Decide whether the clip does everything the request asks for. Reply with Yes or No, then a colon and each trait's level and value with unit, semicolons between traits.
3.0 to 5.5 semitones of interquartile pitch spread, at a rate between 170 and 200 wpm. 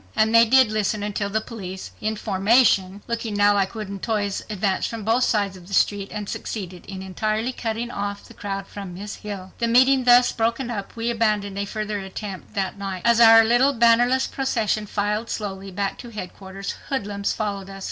No: narrow, 2.6 semitones; average, 185 wpm